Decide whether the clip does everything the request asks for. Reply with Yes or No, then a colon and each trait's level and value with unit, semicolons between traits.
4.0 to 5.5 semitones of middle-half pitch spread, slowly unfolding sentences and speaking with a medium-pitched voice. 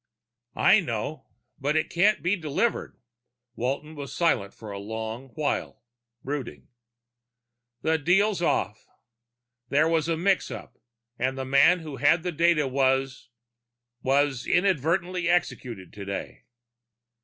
Yes: average, 4.6 semitones; slow, 120 wpm; medium, 145 Hz